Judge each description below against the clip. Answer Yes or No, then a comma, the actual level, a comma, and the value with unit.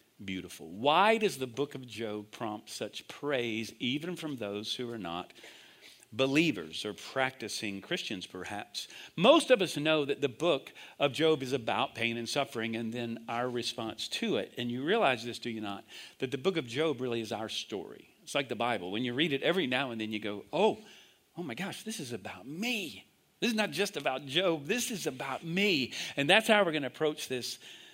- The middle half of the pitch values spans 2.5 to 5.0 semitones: No, wide, 5.6 semitones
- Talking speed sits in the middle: No, fast, 210 wpm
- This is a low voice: Yes, low, 130 Hz